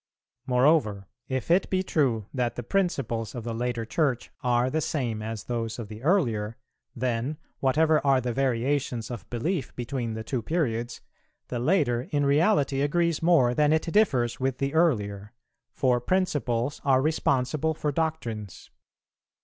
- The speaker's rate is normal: Yes, average, 150 wpm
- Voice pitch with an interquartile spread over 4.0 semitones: Yes, average, 4.7 semitones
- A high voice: No, low, 130 Hz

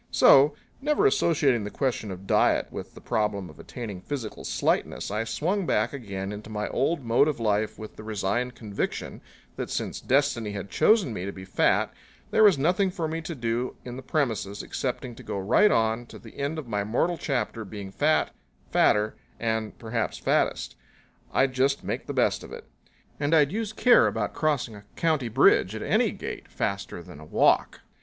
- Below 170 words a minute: No, average, 190 wpm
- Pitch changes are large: Yes, wide, 5.7 semitones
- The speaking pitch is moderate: No, low, 120 Hz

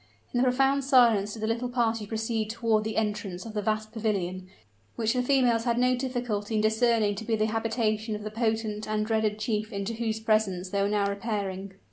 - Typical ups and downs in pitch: No, narrow, 1.8 semitones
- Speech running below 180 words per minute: No, average, 200 wpm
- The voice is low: No, high, 220 Hz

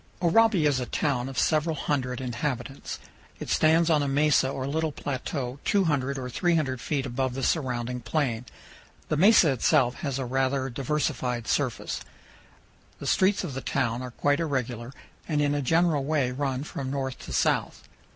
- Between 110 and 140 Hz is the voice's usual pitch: Yes, low, 135 Hz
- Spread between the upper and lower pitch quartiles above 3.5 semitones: No, average, 3.2 semitones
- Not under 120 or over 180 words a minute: Yes, average, 165 wpm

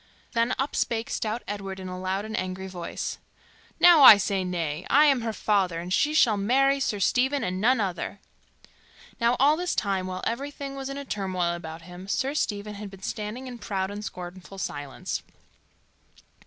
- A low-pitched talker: No, high, 205 Hz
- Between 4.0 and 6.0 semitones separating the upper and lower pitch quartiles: Yes, wide, 5.5 semitones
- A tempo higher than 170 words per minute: Yes, average, 180 wpm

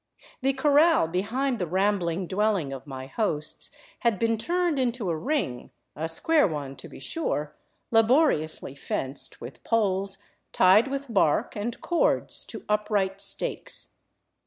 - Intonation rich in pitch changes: Yes, wide, 7.4 semitones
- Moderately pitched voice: No, high, 205 Hz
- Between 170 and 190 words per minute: No, average, 140 wpm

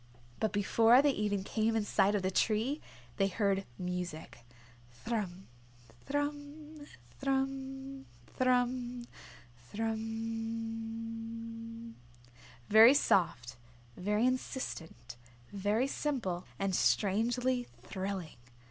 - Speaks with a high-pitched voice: Yes, high, 225 Hz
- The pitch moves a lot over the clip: No, average, 4.3 semitones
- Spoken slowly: Yes, slow, 85 wpm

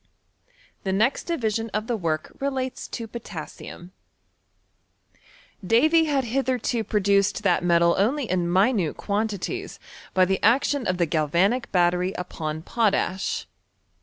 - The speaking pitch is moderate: No, high, 205 Hz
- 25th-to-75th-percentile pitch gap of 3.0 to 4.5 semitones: No, average, 5.3 semitones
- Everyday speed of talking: No, slow, 125 wpm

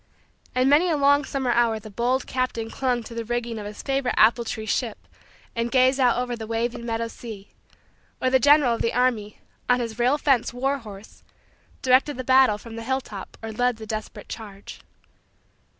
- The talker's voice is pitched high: Yes, high, 240 Hz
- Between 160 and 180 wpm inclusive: No, average, 190 wpm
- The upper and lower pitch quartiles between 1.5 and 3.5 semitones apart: Yes, narrow, 2.5 semitones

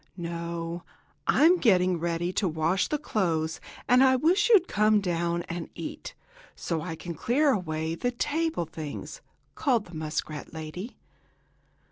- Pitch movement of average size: No, wide, 6.8 semitones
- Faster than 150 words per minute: No, average, 140 wpm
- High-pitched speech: No, medium, 175 Hz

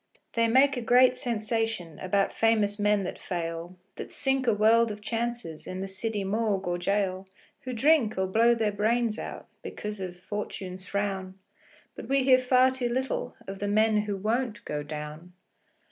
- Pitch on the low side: No, high, 210 Hz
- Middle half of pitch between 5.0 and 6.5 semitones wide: No, average, 3.8 semitones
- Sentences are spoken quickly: No, average, 175 wpm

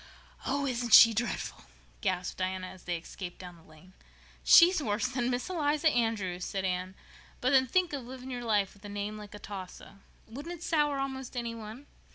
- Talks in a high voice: Yes, high, 230 Hz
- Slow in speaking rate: No, average, 195 wpm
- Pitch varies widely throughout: Yes, wide, 5.8 semitones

